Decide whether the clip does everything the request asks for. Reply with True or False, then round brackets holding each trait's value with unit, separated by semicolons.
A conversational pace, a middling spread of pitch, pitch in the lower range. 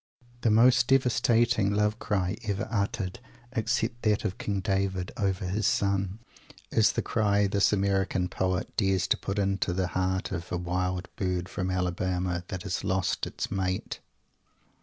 False (155 wpm; 2.3 semitones; 95 Hz)